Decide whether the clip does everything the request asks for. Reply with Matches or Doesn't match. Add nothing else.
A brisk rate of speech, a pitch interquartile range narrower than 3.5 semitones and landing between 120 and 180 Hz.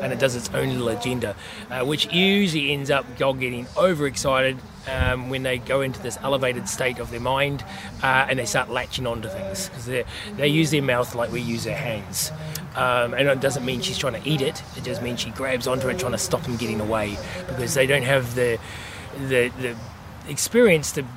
Matches